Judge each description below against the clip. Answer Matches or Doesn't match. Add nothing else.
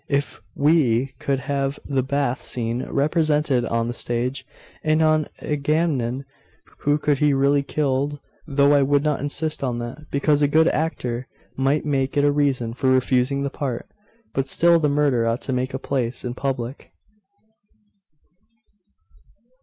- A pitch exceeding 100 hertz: Matches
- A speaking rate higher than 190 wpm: Doesn't match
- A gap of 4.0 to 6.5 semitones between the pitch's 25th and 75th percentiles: Doesn't match